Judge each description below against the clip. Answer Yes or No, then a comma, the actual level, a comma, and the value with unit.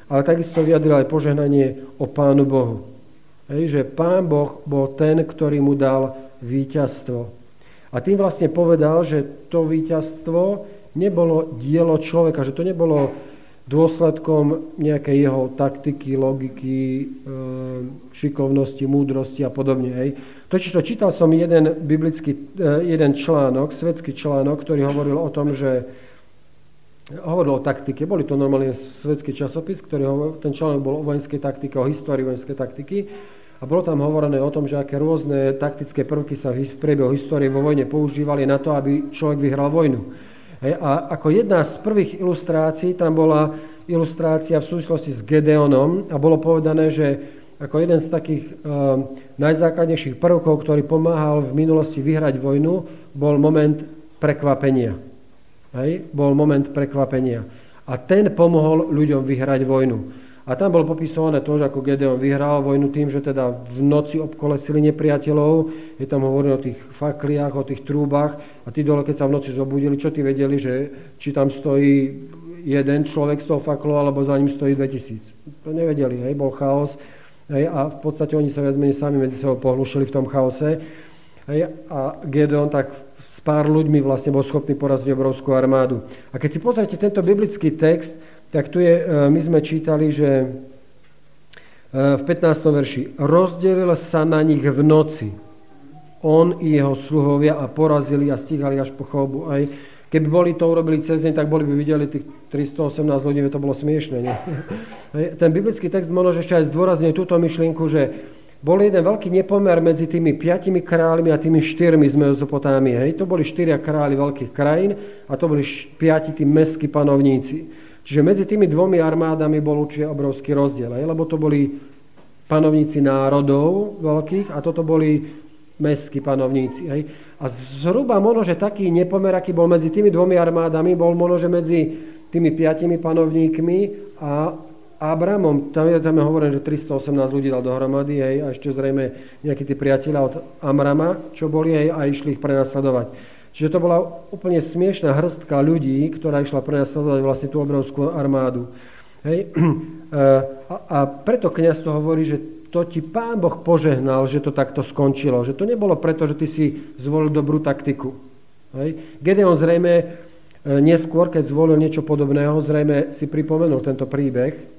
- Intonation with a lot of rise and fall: No, average, 2.7 semitones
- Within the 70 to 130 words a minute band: No, average, 160 wpm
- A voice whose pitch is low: No, medium, 150 Hz